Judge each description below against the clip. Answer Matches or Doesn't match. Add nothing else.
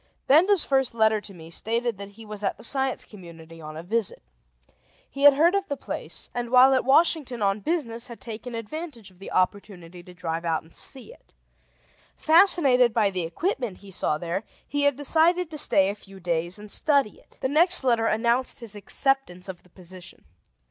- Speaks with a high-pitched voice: Matches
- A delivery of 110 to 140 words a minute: Doesn't match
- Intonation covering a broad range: Matches